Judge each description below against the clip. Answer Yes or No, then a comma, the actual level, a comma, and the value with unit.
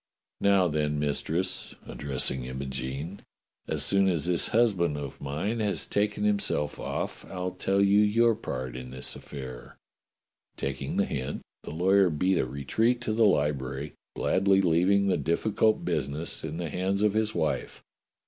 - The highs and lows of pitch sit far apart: Yes, wide, 5.8 semitones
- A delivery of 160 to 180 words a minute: No, average, 150 wpm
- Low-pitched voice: Yes, very low, 85 Hz